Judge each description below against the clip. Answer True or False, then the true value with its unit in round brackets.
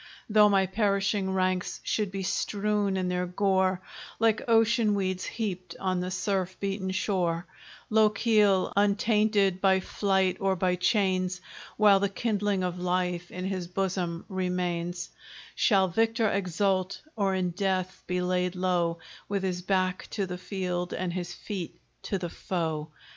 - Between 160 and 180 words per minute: False (145 wpm)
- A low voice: False (190 Hz)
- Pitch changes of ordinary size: False (1.8 semitones)